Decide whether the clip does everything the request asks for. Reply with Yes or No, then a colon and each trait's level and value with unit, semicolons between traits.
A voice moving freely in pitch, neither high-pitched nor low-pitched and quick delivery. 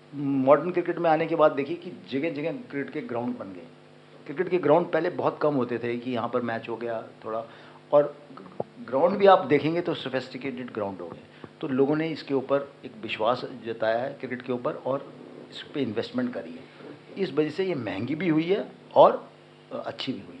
No: average, 4.9 semitones; medium, 145 Hz; fast, 210 wpm